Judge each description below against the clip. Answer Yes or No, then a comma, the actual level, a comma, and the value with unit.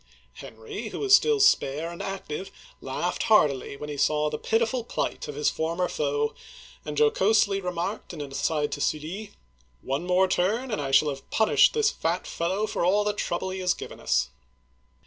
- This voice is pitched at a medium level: Yes, medium, 175 Hz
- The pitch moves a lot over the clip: Yes, wide, 5.8 semitones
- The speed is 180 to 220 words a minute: Yes, average, 190 wpm